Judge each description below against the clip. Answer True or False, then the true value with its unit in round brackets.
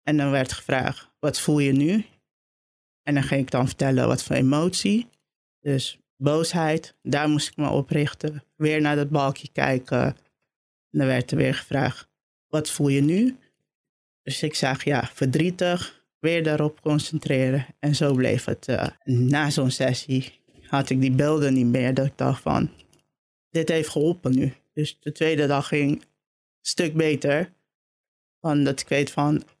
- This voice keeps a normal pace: True (170 wpm)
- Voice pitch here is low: False (145 Hz)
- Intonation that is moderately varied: False (2.3 semitones)